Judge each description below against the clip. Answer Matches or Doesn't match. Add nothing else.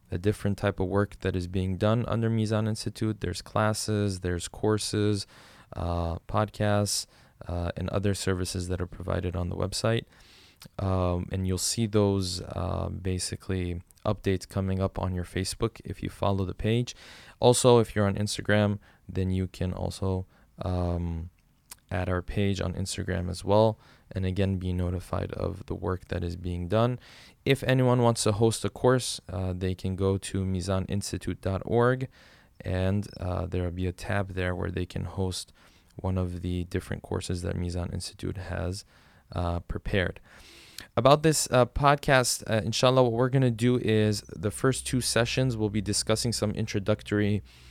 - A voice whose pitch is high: Doesn't match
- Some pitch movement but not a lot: Matches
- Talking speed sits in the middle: Matches